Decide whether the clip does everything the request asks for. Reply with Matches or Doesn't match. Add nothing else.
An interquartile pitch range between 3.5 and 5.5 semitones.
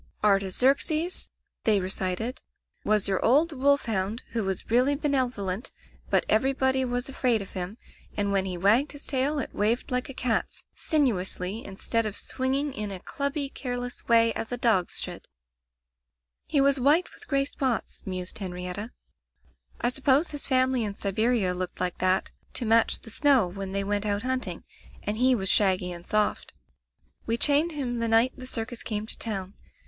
Matches